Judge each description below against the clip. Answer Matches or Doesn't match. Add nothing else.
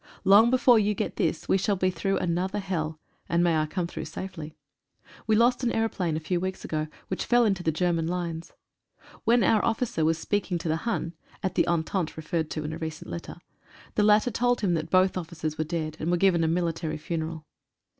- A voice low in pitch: Doesn't match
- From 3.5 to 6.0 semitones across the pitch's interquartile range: Matches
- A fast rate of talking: Matches